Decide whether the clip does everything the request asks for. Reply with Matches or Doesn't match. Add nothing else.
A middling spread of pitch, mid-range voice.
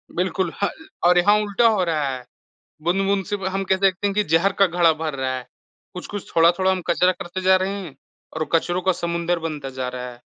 Matches